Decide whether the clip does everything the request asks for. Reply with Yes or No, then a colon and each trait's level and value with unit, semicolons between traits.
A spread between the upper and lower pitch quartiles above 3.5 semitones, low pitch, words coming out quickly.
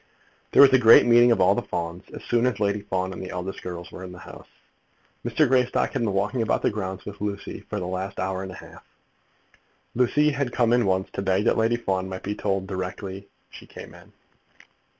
Yes: average, 4.1 semitones; low, 100 Hz; fast, 225 wpm